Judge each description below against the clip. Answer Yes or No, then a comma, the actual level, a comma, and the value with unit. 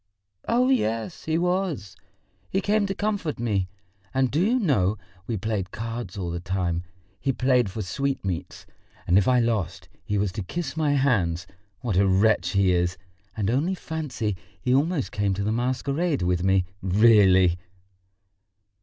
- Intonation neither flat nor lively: No, wide, 7.1 semitones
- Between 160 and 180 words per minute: Yes, average, 165 wpm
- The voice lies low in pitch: Yes, low, 115 Hz